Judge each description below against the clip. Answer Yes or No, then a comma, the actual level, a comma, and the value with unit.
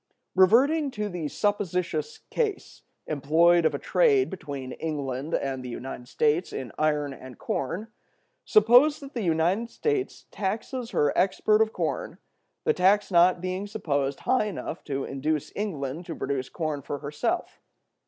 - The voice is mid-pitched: Yes, medium, 170 Hz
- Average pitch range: No, wide, 6.9 semitones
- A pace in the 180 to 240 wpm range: No, average, 145 wpm